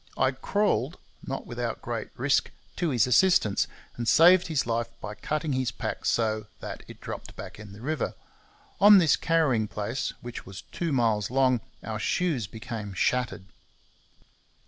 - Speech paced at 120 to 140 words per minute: No, average, 155 wpm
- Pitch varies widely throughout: Yes, wide, 6.2 semitones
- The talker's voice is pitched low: Yes, low, 125 Hz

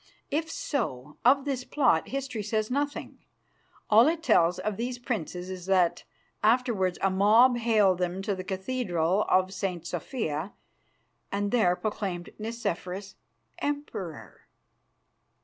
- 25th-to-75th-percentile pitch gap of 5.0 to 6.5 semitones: Yes, average, 5.3 semitones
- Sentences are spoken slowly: Yes, slow, 125 wpm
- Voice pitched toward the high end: Yes, high, 205 Hz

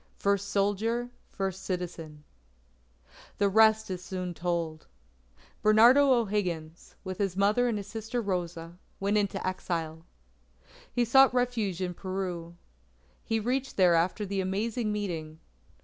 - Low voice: No, high, 195 Hz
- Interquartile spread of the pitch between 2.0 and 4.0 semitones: Yes, average, 3.7 semitones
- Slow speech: Yes, slow, 125 wpm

